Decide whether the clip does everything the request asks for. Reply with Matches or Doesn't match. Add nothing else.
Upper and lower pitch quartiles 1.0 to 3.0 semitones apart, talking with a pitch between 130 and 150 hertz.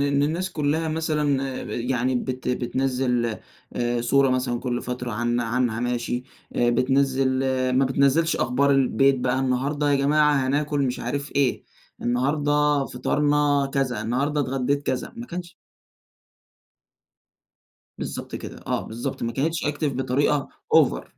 Matches